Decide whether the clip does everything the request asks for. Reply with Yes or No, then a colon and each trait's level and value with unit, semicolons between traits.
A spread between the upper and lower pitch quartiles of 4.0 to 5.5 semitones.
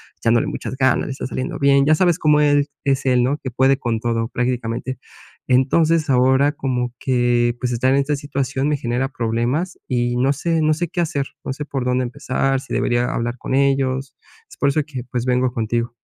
No: narrow, 2.5 semitones